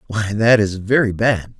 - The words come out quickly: No, average, 190 wpm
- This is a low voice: Yes, low, 105 Hz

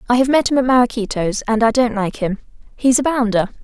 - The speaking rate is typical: No, fast, 230 wpm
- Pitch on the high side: Yes, high, 235 Hz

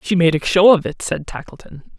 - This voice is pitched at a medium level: Yes, medium, 175 Hz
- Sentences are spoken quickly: Yes, fast, 240 wpm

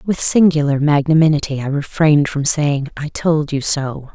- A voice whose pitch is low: No, medium, 150 Hz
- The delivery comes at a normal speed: Yes, average, 160 wpm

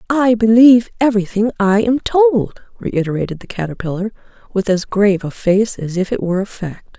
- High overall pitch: Yes, high, 210 Hz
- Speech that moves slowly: No, average, 170 wpm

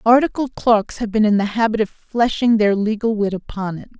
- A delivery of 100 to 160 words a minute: No, fast, 210 wpm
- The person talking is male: No, female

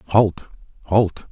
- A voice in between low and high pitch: No, very low, 95 Hz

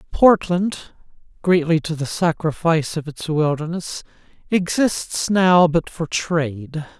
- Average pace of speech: No, slow, 110 wpm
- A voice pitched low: No, medium, 165 Hz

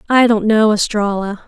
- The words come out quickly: No, average, 165 wpm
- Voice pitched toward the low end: No, high, 215 Hz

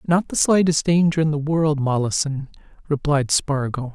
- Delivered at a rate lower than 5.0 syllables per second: Yes, 4.7 syllables/s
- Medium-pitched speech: Yes, medium, 150 Hz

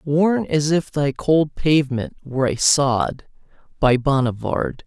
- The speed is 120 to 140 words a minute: Yes, slow, 135 wpm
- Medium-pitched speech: Yes, medium, 145 Hz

